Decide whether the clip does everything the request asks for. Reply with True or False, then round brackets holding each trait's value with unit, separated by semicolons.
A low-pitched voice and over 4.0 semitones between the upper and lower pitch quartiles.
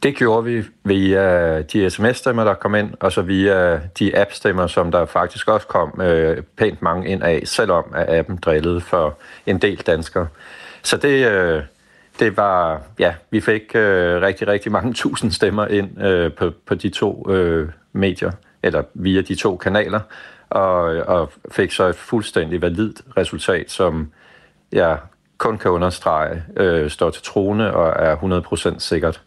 False (90 Hz; 3.3 semitones)